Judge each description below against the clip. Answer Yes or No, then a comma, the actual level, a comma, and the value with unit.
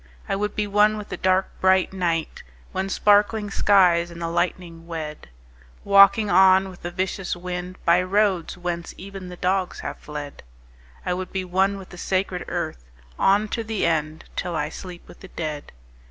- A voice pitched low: No, medium, 185 Hz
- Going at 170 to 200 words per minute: Yes, average, 180 wpm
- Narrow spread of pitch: Yes, narrow, 2.3 semitones